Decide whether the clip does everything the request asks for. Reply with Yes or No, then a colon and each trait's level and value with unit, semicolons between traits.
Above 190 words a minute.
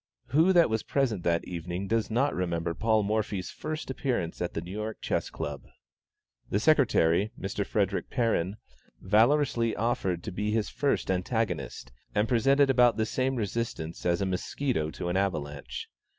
No: average, 160 wpm